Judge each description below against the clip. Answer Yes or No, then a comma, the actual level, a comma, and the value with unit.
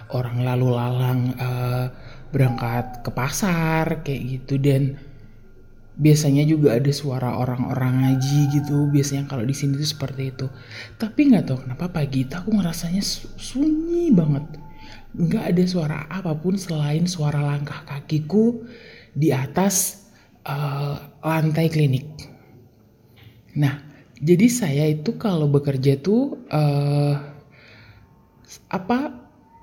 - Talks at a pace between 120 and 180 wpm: No, average, 110 wpm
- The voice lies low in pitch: No, medium, 145 Hz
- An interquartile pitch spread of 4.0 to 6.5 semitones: Yes, average, 4.3 semitones